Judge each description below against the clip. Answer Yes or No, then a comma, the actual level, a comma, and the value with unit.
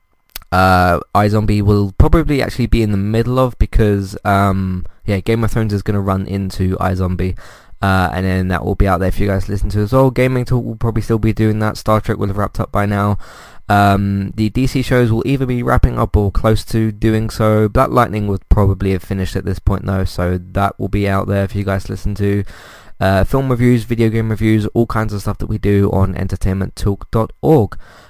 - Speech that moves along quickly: Yes, fast, 220 wpm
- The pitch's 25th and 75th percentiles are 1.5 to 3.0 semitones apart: Yes, narrow, 2.6 semitones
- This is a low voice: Yes, low, 100 Hz